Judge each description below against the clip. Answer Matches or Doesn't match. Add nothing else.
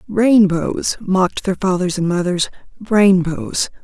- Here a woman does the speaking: Matches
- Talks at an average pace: Doesn't match